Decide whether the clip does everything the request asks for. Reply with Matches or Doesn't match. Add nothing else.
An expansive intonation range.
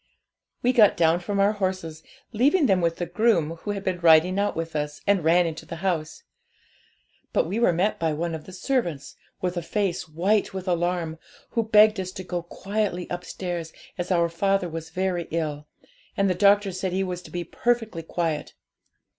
Doesn't match